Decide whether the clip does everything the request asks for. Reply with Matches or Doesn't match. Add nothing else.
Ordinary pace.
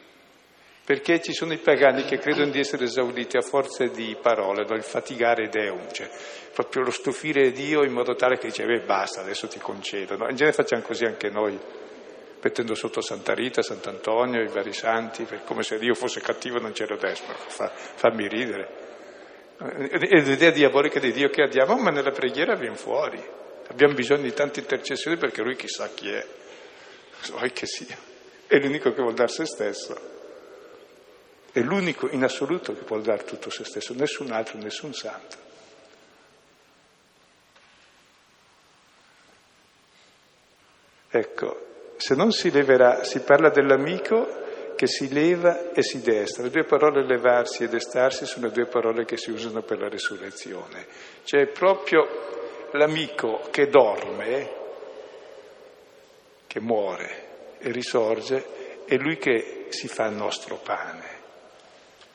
Matches